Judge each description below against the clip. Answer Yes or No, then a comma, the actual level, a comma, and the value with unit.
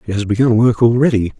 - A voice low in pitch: Yes, low, 110 Hz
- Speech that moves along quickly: Yes, fast, 215 wpm